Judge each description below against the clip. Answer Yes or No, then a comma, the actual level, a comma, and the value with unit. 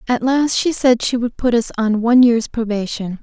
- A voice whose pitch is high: Yes, high, 235 Hz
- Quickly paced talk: Yes, fast, 225 wpm